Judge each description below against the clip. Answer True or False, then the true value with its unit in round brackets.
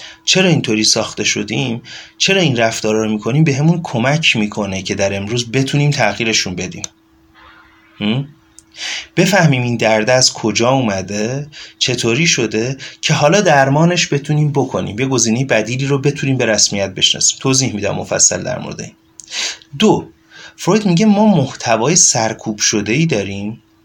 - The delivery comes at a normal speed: True (140 wpm)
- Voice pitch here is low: True (130 Hz)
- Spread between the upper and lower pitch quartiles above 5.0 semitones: True (5.5 semitones)